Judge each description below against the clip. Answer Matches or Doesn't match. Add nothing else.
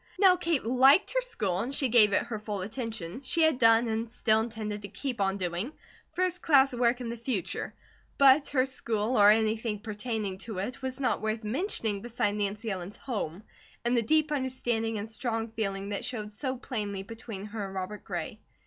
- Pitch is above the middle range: Matches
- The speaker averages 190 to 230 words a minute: Matches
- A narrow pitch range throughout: Doesn't match